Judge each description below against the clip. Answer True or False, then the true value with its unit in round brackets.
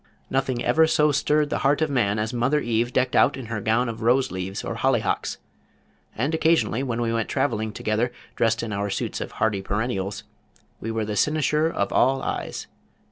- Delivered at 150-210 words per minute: True (190 wpm)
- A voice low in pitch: True (120 Hz)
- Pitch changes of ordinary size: True (3.8 semitones)